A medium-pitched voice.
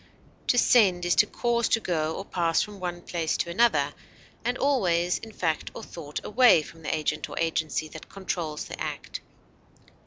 Yes: medium, 175 Hz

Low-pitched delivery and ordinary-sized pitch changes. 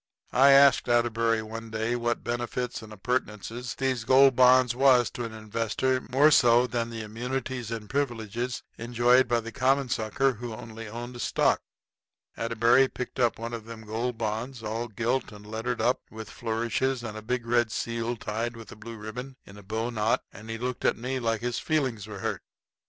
No: low, 120 Hz; narrow, 2.0 semitones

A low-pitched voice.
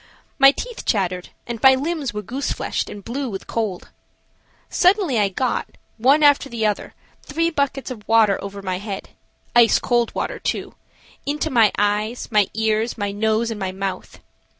No: high, 225 Hz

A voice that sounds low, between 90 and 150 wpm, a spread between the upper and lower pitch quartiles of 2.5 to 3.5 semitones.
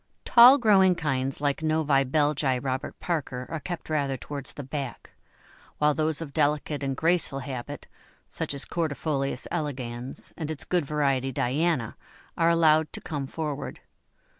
No: medium, 145 Hz; average, 145 wpm; average, 2.8 semitones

